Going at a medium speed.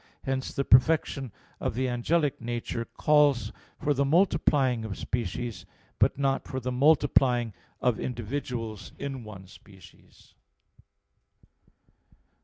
No: slow, 115 wpm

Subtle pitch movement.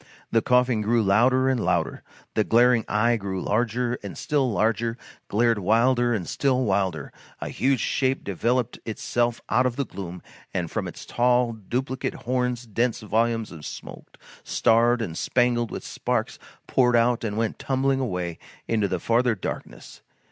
No: average, 3.0 semitones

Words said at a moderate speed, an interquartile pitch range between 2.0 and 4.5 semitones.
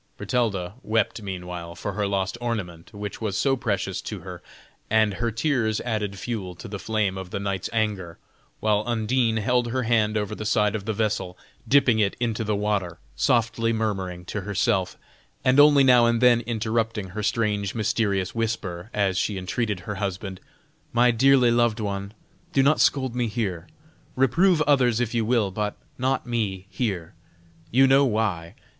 Yes: average, 170 wpm; average, 3.3 semitones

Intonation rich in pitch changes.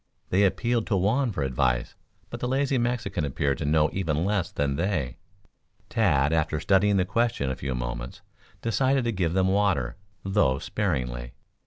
Yes: wide, 7.1 semitones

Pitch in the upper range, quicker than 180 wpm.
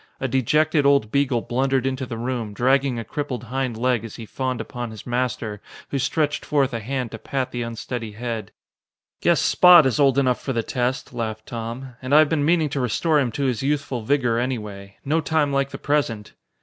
No: low, 130 Hz; fast, 205 wpm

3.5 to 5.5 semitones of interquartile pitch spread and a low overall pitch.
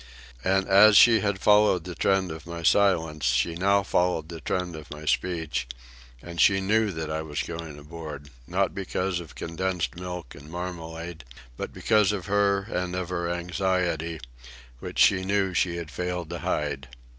No: average, 2.9 semitones; very low, 90 Hz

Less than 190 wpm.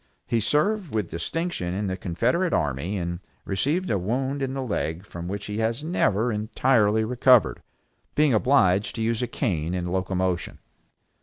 Yes: average, 160 wpm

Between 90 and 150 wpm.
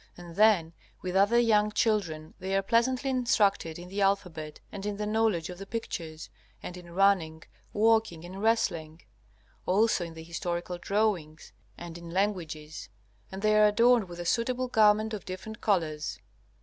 No: average, 160 wpm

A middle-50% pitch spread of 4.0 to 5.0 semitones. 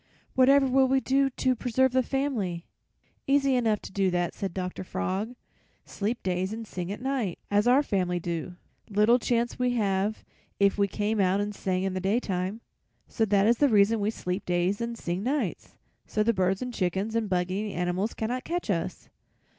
Yes: average, 4.7 semitones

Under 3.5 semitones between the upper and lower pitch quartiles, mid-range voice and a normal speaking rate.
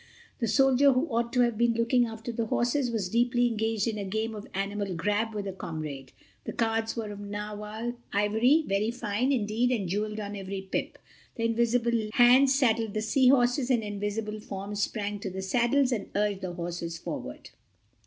No: average, 2.9 semitones; high, 220 Hz; average, 185 wpm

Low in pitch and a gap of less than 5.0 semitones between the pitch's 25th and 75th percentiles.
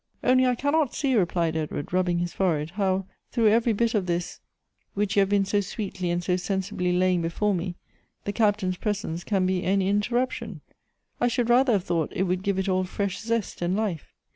No: high, 195 Hz; average, 3.2 semitones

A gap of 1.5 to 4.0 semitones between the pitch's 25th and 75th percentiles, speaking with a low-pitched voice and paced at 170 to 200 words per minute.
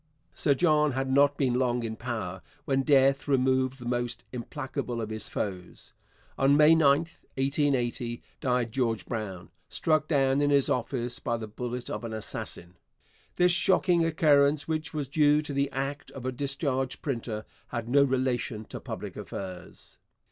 No: average, 3.3 semitones; low, 130 Hz; average, 160 wpm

